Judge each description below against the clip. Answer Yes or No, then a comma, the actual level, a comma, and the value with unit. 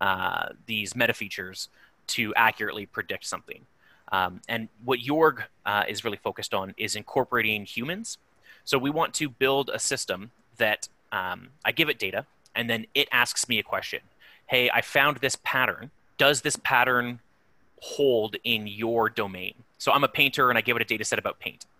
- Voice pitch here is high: No, low, 120 Hz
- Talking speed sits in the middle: Yes, average, 180 wpm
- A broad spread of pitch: No, average, 3.7 semitones